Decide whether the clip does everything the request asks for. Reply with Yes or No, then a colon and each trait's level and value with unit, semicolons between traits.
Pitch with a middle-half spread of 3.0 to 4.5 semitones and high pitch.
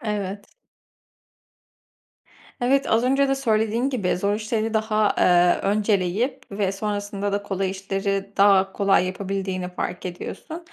No: narrow, 2.4 semitones; high, 205 Hz